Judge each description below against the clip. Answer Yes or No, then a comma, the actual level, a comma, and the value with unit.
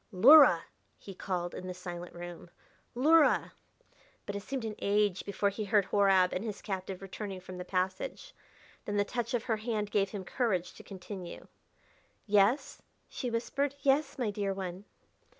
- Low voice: No, high, 200 Hz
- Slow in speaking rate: No, average, 165 wpm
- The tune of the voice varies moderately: Yes, average, 3.4 semitones